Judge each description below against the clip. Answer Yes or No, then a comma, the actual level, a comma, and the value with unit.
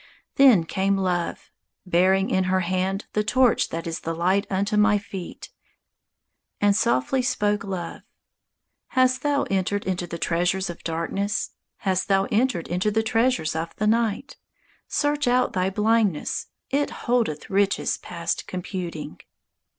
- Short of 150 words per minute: Yes, average, 140 wpm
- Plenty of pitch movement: No, average, 3.8 semitones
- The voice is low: No, high, 195 Hz